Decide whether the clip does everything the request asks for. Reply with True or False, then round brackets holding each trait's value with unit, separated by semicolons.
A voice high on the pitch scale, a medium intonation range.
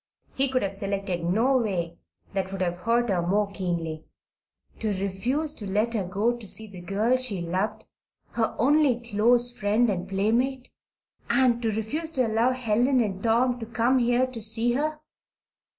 True (220 Hz; 3.8 semitones)